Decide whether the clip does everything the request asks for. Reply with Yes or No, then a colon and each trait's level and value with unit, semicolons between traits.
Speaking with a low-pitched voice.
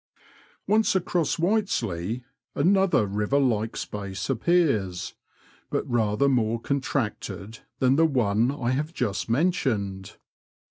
Yes: low, 125 Hz